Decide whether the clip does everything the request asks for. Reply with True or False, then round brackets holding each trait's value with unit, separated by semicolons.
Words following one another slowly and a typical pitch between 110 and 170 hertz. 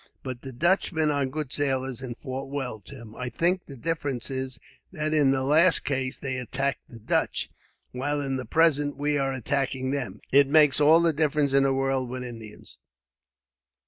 False (180 wpm; 135 Hz)